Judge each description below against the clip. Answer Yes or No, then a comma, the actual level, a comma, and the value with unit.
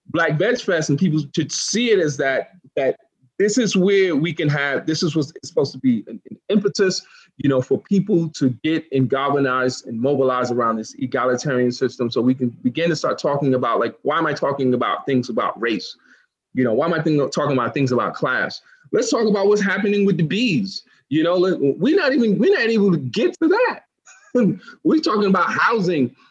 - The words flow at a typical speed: No, fast, 210 wpm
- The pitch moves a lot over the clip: Yes, wide, 7.3 semitones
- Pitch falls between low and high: Yes, medium, 160 Hz